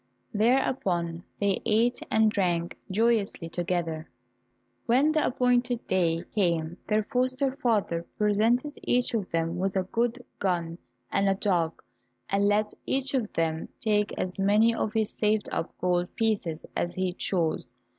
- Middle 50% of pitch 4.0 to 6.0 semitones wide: Yes, average, 4.9 semitones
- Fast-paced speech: No, average, 145 wpm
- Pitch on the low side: No, high, 205 Hz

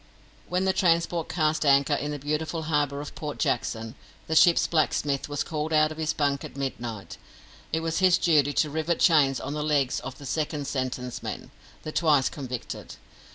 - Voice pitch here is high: No, medium, 150 Hz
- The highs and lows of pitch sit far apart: No, narrow, 2.4 semitones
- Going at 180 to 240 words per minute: Yes, average, 185 wpm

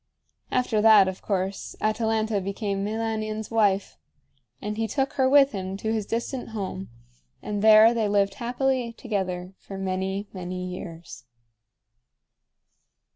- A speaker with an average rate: No, slow, 130 wpm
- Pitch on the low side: No, high, 210 Hz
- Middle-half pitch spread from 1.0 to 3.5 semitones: Yes, narrow, 2.6 semitones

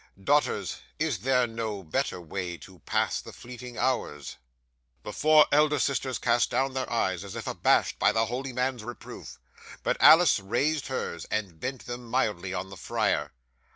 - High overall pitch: No, low, 120 Hz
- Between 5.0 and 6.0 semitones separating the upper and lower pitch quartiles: Yes, wide, 5.4 semitones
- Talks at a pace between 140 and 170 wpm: Yes, average, 165 wpm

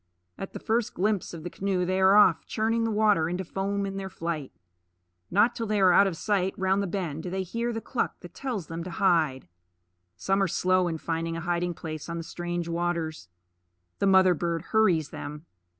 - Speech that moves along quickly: Yes, fast, 210 wpm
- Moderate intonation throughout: Yes, average, 3.1 semitones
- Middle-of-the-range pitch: Yes, medium, 180 Hz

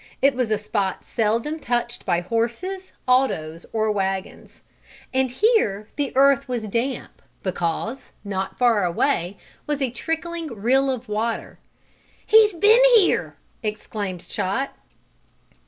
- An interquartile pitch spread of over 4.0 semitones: Yes, average, 5.2 semitones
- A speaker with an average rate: No, slow, 120 wpm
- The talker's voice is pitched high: Yes, high, 235 Hz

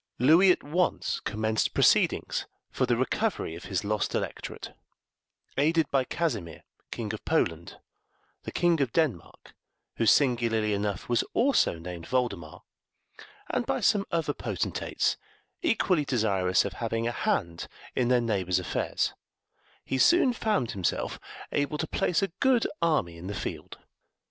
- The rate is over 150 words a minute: No, average, 140 wpm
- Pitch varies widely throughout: Yes, wide, 8.3 semitones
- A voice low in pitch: Yes, low, 120 Hz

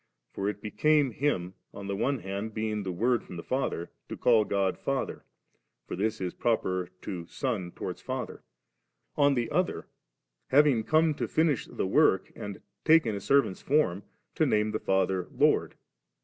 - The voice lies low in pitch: Yes, low, 110 Hz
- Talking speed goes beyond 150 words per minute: Yes, average, 165 wpm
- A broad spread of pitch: Yes, wide, 6.2 semitones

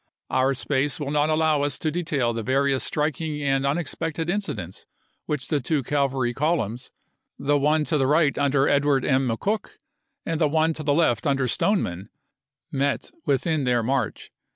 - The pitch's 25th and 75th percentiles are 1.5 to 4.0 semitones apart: Yes, average, 2.8 semitones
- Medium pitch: Yes, medium, 145 Hz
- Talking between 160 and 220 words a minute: Yes, average, 175 wpm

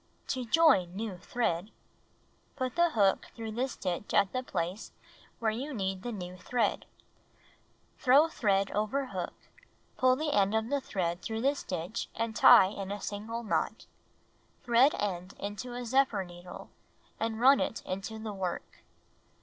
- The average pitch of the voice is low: No, high, 220 Hz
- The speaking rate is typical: Yes, average, 165 wpm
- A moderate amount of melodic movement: Yes, average, 4.6 semitones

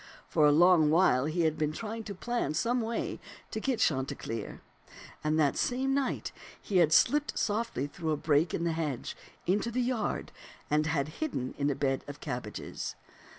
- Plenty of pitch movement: Yes, wide, 7.3 semitones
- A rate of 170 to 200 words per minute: Yes, average, 180 wpm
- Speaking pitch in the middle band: Yes, medium, 160 Hz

